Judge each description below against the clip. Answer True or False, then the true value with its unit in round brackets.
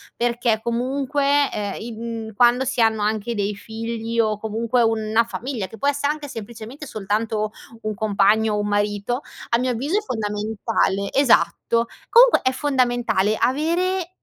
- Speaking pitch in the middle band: False (230 Hz)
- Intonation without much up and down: False (3.3 semitones)